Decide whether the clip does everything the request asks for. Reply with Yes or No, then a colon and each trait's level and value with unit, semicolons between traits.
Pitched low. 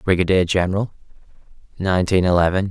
Yes: very low, 90 Hz